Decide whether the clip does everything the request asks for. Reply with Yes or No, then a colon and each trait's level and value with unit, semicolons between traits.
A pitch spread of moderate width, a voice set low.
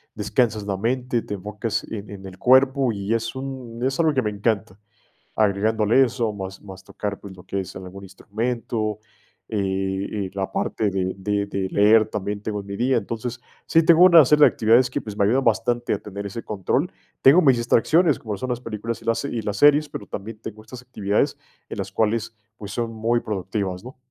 Yes: average, 3.4 semitones; low, 110 Hz